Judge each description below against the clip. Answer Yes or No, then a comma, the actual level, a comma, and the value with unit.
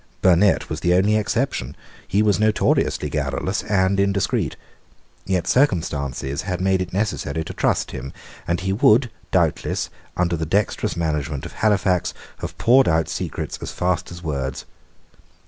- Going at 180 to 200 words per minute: No, average, 145 wpm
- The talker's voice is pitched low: Yes, very low, 90 Hz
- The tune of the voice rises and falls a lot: No, average, 4.2 semitones